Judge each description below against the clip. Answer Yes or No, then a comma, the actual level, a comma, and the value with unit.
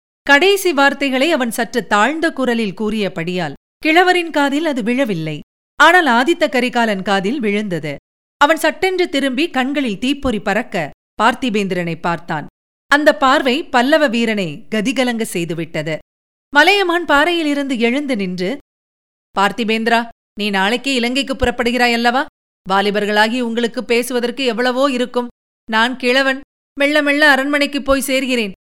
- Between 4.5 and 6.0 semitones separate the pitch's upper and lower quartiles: Yes, average, 5.2 semitones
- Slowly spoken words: No, average, 110 wpm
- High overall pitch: Yes, high, 245 Hz